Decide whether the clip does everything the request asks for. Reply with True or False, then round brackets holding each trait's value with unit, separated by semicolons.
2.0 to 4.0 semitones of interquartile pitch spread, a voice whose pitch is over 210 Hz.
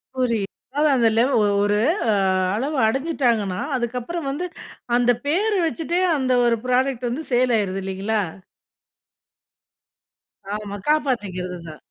False (5.1 semitones; 245 Hz)